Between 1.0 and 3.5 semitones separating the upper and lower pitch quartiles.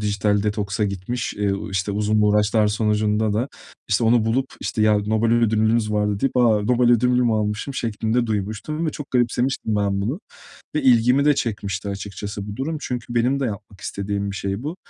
Yes: average, 2.9 semitones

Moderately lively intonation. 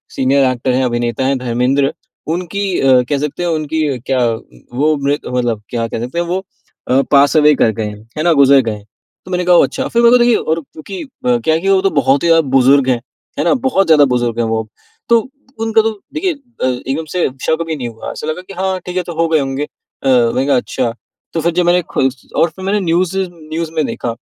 No: wide, 5.8 semitones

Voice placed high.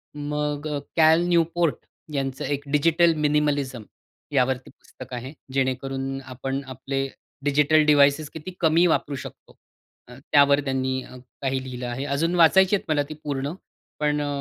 No: medium, 145 Hz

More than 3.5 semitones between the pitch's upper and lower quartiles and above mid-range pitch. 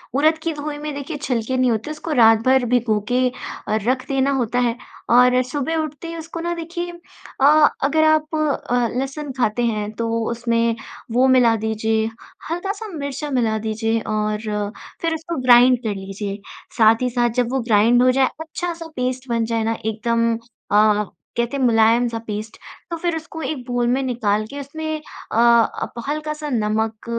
Yes: average, 4.8 semitones; high, 245 Hz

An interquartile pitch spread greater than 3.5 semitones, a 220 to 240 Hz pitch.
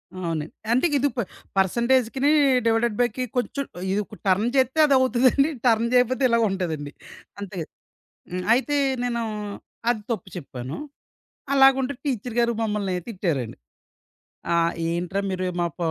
Yes: wide, 5.6 semitones; high, 225 Hz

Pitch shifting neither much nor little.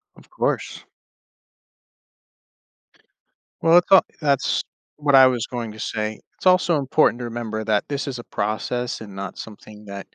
Yes: average, 4.7 semitones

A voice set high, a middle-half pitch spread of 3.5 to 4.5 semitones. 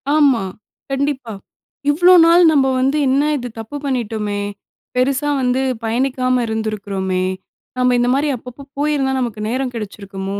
Yes: very high, 250 Hz; average, 3.9 semitones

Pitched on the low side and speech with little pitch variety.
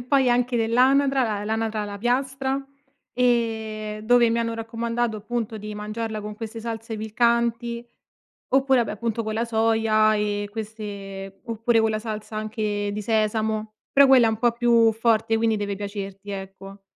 No: high, 225 Hz; narrow, 1.8 semitones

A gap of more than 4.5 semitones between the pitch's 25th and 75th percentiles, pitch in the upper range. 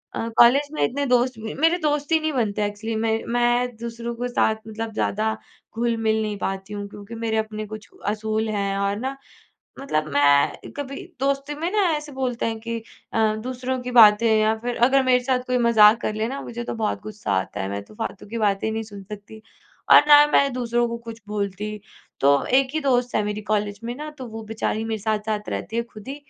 No: average, 2.9 semitones; high, 225 Hz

